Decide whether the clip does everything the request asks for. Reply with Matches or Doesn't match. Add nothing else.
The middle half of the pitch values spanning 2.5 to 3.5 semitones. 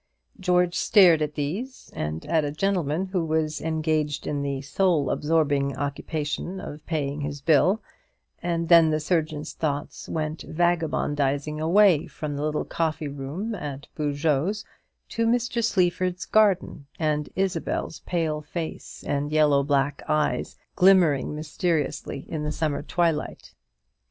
Matches